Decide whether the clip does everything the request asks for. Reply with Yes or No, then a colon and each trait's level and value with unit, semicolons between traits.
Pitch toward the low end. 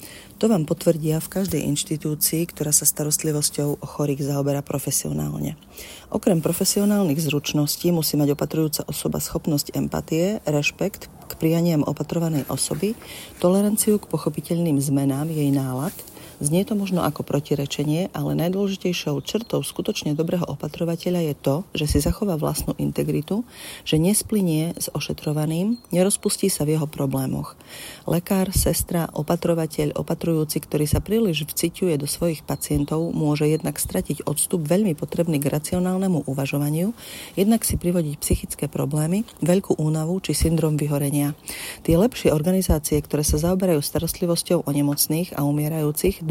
No: medium, 155 Hz